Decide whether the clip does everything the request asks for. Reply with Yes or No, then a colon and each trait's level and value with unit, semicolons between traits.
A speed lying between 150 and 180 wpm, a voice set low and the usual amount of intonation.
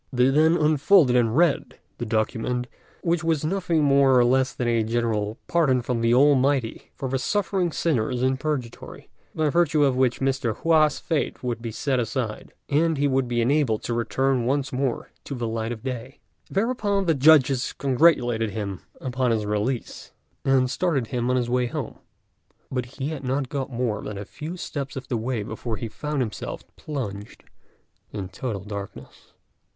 Yes: average, 175 wpm; low, 130 Hz; average, 3.8 semitones